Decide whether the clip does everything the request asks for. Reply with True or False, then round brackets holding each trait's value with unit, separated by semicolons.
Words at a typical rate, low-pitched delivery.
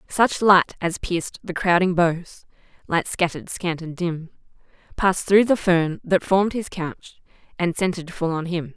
False (170 wpm; 175 Hz)